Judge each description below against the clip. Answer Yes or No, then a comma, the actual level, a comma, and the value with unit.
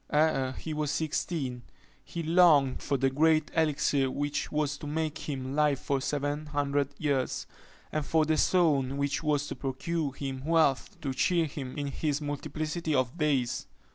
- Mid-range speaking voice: Yes, medium, 145 Hz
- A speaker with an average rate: Yes, average, 165 wpm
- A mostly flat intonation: Yes, narrow, 2.3 semitones